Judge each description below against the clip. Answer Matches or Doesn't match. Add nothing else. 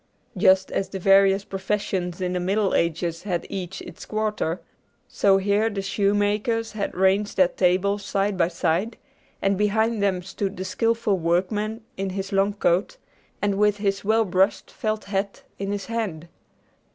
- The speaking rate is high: Doesn't match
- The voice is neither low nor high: Doesn't match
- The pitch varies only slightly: Matches